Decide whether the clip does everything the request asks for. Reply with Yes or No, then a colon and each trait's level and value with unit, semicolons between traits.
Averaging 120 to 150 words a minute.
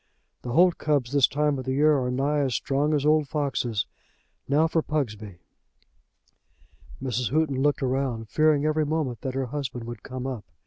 No: average, 175 wpm